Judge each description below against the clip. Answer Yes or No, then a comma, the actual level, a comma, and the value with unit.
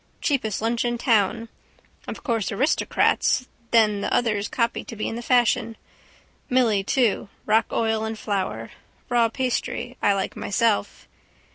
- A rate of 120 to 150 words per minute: Yes, average, 140 wpm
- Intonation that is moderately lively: No, narrow, 2.3 semitones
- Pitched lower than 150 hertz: No, high, 225 Hz